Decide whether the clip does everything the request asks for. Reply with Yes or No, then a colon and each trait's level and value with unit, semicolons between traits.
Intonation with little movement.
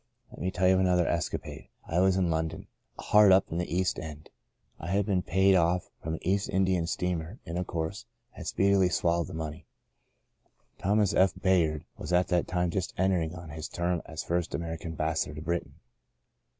Yes: narrow, 2.3 semitones